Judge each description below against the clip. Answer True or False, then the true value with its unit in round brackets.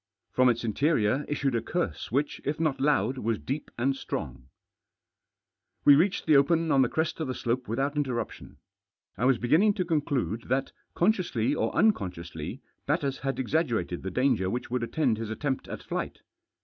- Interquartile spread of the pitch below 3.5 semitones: False (4.3 semitones)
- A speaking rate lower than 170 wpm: False (175 wpm)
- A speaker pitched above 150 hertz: False (135 Hz)